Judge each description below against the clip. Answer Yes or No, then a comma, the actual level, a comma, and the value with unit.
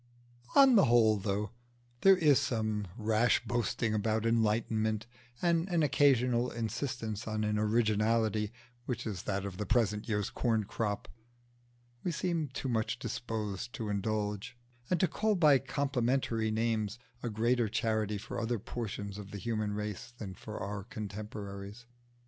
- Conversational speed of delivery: Yes, average, 145 wpm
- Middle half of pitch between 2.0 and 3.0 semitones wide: Yes, narrow, 2.5 semitones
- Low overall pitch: Yes, low, 110 Hz